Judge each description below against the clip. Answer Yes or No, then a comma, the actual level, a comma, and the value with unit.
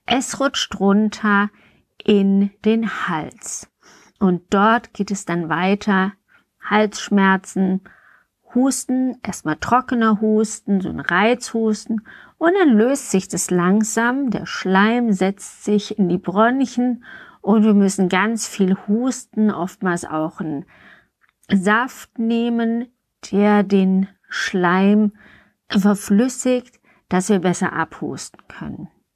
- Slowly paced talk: Yes, slow, 110 wpm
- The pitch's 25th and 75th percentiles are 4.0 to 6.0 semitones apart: No, average, 3.4 semitones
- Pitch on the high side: Yes, high, 210 Hz